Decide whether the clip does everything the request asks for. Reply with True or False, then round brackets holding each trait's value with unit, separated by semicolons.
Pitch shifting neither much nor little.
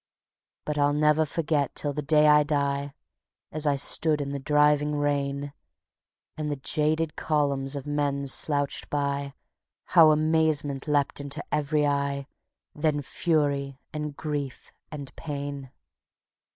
False (1.2 semitones)